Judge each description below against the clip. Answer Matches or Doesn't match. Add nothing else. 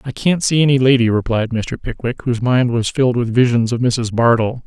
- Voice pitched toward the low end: Matches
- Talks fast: Matches